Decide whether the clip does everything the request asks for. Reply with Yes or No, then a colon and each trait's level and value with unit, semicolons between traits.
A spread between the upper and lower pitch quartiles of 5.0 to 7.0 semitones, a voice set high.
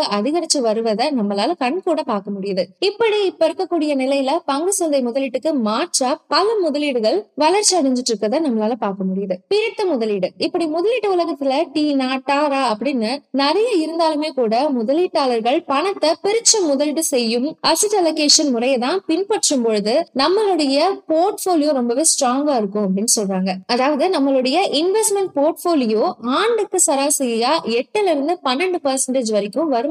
Yes: wide, 5.6 semitones; very high, 290 Hz